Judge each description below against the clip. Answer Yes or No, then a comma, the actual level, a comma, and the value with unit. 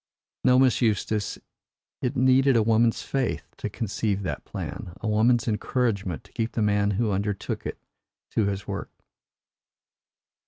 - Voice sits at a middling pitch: No, low, 110 Hz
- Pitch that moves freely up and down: No, average, 3.2 semitones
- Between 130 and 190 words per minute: Yes, average, 145 wpm